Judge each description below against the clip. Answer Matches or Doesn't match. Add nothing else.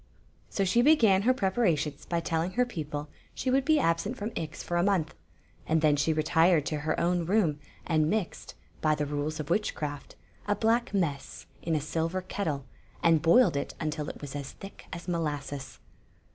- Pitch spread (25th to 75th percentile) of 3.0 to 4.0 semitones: Doesn't match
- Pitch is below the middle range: Doesn't match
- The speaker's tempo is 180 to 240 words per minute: Matches